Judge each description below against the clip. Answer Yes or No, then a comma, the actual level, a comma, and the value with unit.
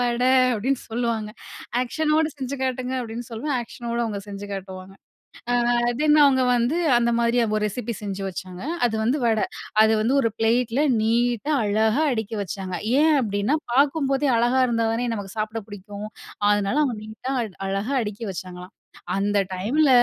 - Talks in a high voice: Yes, high, 230 Hz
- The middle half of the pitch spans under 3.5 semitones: No, average, 3.9 semitones